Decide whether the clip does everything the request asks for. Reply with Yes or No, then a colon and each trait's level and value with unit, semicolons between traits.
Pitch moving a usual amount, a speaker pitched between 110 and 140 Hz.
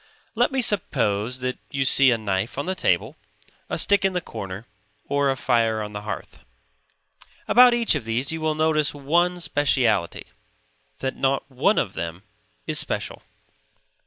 No: wide, 6.2 semitones; low, 135 Hz